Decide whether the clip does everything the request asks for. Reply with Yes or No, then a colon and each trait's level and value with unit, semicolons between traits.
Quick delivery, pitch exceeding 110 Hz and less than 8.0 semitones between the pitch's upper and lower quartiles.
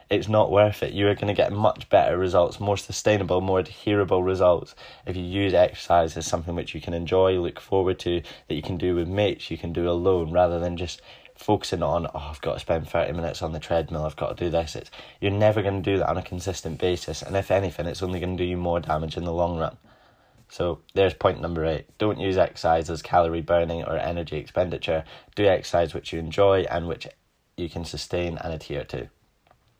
No: fast, 230 wpm; very low, 90 Hz; narrow, 2.4 semitones